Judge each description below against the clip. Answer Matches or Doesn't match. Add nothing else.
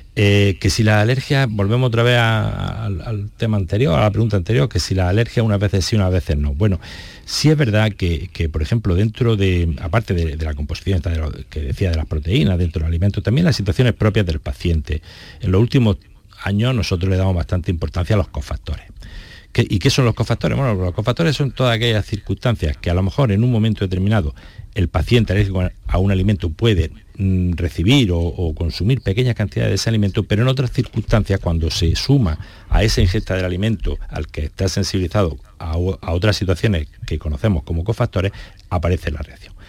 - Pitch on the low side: Matches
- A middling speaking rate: Doesn't match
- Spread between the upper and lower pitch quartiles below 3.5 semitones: Doesn't match